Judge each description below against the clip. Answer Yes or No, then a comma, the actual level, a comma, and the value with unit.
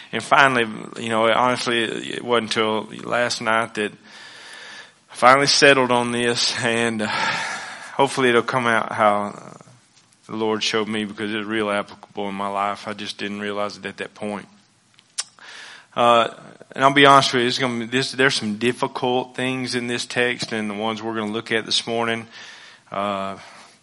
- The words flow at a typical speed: Yes, average, 180 wpm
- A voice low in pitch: Yes, low, 115 Hz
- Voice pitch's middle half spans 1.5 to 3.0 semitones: Yes, average, 2.7 semitones